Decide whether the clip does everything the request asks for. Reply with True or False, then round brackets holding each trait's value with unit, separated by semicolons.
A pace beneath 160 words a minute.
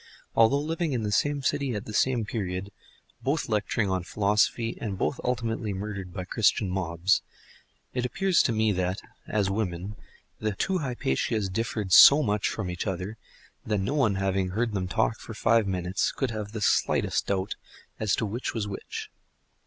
False (175 wpm)